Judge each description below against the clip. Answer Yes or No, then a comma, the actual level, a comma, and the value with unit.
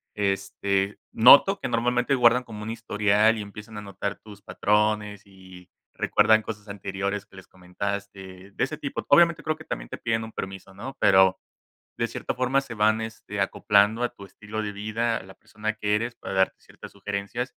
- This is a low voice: Yes, low, 105 Hz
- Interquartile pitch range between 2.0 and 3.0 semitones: Yes, narrow, 2.5 semitones